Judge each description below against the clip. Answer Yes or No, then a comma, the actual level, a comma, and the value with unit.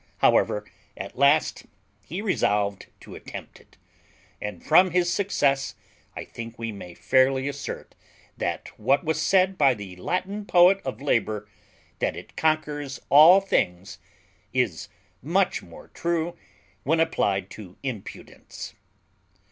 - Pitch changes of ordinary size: No, wide, 8.2 semitones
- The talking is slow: Yes, slow, 125 wpm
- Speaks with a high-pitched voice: No, medium, 140 Hz